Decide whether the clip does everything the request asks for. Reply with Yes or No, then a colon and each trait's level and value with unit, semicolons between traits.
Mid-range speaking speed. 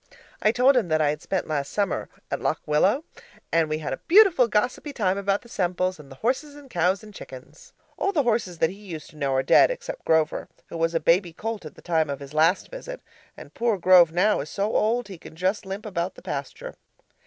No: fast, 235 wpm